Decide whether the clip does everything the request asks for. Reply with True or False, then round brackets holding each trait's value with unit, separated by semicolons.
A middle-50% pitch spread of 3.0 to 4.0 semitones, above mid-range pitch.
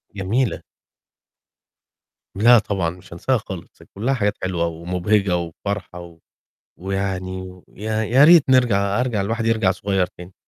False (3.5 semitones; 100 Hz)